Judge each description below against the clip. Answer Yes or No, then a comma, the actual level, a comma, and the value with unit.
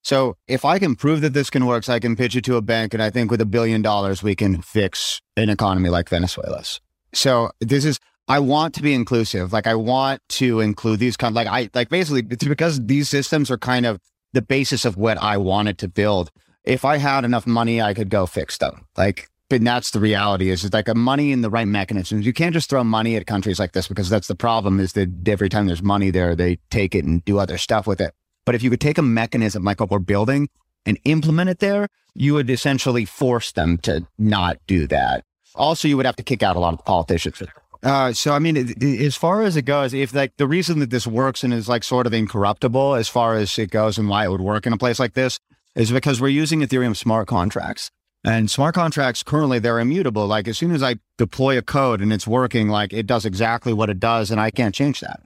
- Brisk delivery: Yes, fast, 250 wpm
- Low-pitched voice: Yes, low, 115 Hz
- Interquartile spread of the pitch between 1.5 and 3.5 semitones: No, average, 4.2 semitones